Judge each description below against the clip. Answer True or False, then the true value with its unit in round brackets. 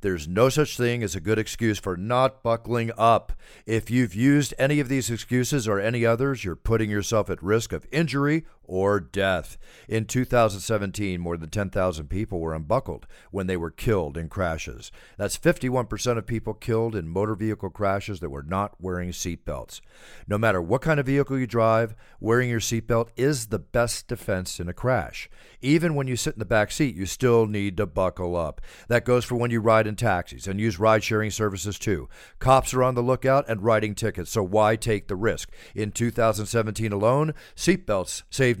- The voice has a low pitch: True (110 Hz)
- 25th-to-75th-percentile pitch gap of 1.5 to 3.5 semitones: False (3.9 semitones)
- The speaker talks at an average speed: True (190 wpm)